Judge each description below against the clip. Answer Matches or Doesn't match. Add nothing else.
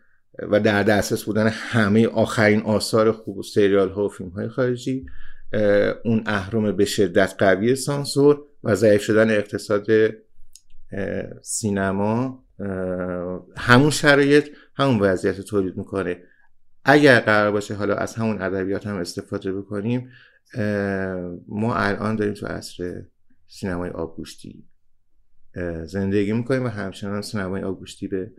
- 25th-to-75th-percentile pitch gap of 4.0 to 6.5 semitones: Doesn't match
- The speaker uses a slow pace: Doesn't match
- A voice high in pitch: Doesn't match